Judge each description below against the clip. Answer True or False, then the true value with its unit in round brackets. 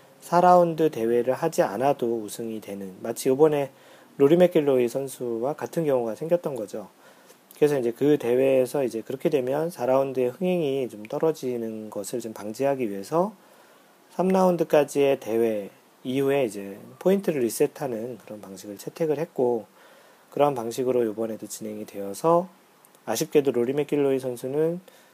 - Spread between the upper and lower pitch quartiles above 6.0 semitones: False (5.5 semitones)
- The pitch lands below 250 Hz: True (135 Hz)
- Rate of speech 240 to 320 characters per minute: False (330 characters per minute)